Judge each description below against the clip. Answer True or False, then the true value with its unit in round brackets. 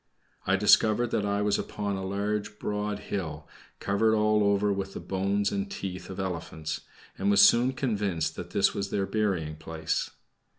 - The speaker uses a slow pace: False (170 wpm)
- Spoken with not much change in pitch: True (1.6 semitones)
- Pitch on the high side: False (100 Hz)